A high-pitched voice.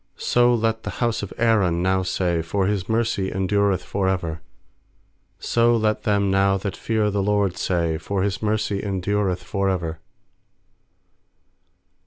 No: low, 100 Hz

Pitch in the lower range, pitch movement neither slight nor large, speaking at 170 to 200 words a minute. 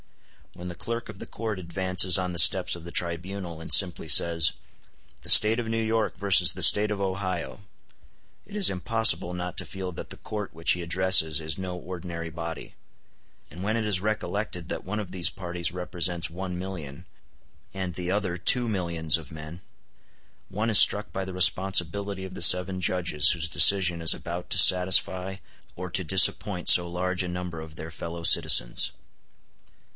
No: very low, 90 Hz; narrow, 2.1 semitones; average, 180 wpm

